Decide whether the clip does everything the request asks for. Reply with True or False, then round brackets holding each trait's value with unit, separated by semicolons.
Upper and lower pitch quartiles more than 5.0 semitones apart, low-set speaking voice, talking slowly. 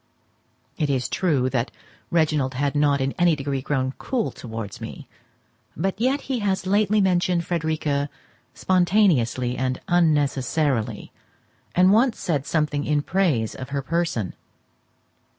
False (5.4 semitones; 150 Hz; 130 wpm)